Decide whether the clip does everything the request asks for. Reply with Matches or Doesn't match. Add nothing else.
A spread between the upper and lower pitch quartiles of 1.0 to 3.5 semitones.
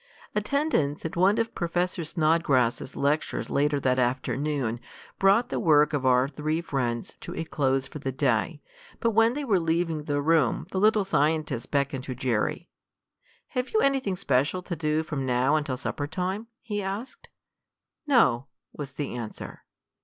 Doesn't match